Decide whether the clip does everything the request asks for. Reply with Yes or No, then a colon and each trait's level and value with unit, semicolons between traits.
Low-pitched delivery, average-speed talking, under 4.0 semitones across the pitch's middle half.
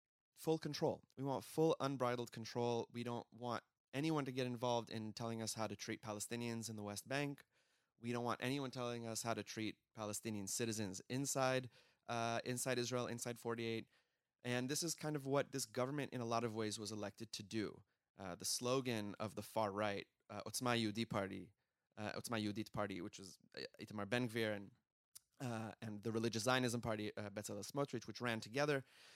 Yes: low, 115 Hz; average, 185 wpm; narrow, 2.6 semitones